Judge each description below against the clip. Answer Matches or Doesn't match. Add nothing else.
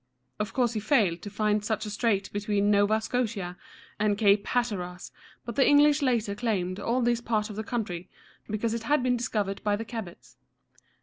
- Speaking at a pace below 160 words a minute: Doesn't match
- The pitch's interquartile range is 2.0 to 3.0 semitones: Matches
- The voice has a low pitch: Doesn't match